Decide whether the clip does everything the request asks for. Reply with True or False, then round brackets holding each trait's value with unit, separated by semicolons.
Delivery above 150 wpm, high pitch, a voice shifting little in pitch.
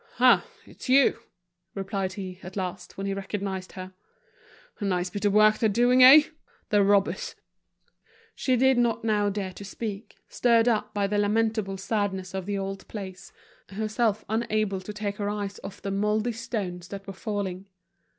True (170 wpm; 205 Hz; 2.1 semitones)